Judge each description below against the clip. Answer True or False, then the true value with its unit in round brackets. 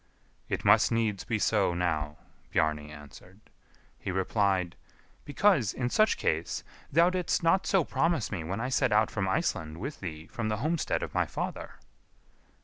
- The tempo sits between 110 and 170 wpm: True (160 wpm)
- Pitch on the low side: True (105 Hz)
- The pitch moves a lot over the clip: True (7.6 semitones)